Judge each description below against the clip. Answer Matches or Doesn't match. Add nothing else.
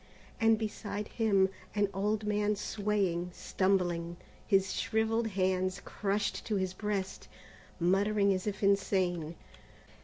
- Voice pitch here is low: Doesn't match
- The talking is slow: Matches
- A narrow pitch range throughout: Matches